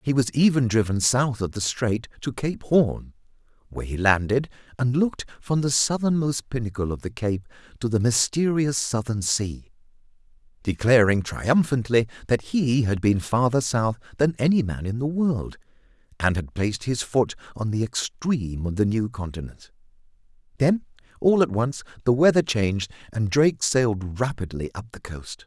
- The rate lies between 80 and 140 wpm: No, average, 160 wpm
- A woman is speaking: No, male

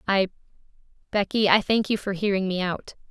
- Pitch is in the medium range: No, high, 195 Hz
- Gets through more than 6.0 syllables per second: No, 5.6 syllables/s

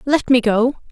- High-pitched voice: Yes, high, 245 Hz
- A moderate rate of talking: Yes, average, 195 wpm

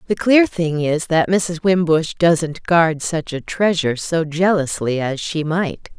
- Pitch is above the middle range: No, medium, 165 Hz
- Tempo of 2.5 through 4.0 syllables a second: Yes, 3.9 syllables/s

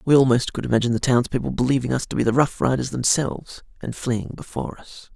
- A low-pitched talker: Yes, low, 125 Hz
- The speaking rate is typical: No, fast, 210 wpm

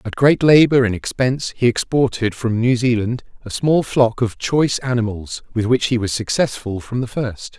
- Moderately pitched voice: No, low, 120 Hz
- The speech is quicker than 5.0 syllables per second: No, 4.9 syllables/s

